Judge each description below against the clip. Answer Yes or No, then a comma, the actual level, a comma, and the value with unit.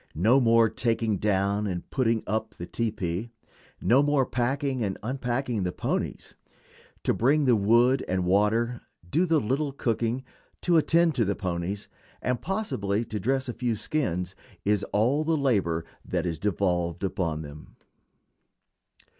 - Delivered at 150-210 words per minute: No, average, 140 wpm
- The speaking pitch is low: Yes, low, 115 Hz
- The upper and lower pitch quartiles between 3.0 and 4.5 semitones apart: No, average, 5.2 semitones